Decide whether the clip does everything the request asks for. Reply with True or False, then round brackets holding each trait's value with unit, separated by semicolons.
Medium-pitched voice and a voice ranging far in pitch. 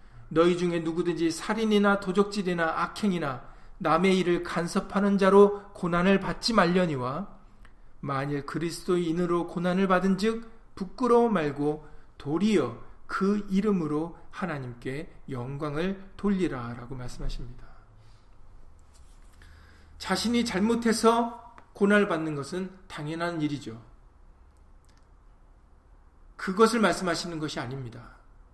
True (165 Hz; 8.2 semitones)